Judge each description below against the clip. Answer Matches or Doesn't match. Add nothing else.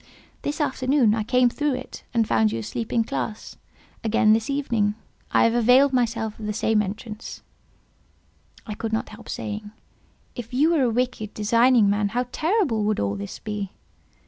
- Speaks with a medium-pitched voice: Doesn't match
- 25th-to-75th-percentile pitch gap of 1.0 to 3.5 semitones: Matches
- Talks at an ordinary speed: Matches